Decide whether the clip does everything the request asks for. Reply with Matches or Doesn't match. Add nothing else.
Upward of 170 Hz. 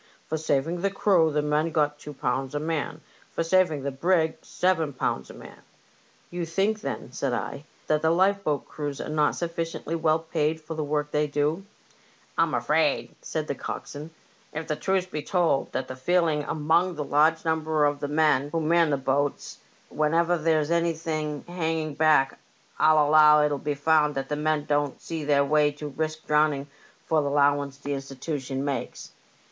Doesn't match